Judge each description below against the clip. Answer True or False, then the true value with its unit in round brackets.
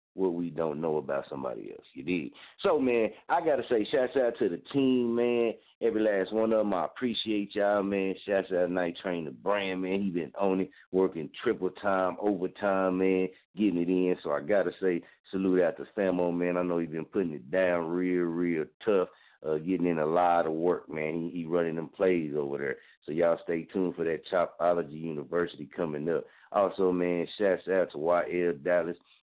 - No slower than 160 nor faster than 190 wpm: False (205 wpm)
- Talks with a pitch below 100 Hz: True (90 Hz)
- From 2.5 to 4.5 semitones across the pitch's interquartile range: False (2.1 semitones)